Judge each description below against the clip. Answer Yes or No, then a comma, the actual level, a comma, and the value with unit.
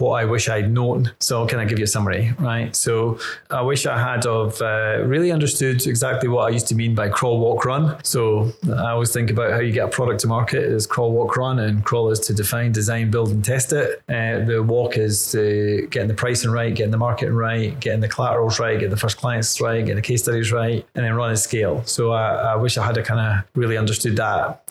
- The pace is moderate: No, fast, 250 wpm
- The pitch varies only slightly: Yes, narrow, 1.7 semitones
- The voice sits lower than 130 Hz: Yes, low, 115 Hz